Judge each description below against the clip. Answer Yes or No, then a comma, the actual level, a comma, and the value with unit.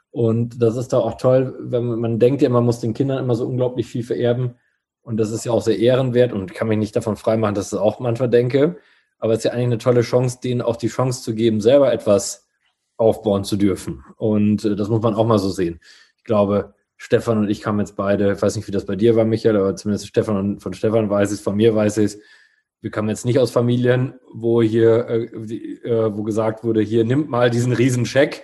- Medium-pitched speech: No, low, 115 Hz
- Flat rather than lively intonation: Yes, narrow, 2.3 semitones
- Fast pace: Yes, fast, 240 wpm